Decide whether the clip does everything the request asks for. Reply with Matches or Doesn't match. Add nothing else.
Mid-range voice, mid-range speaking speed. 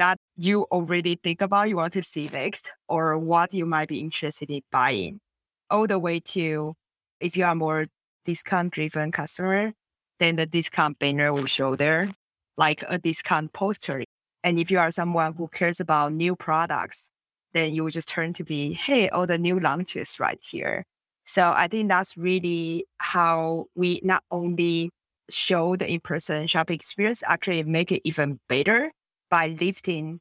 Matches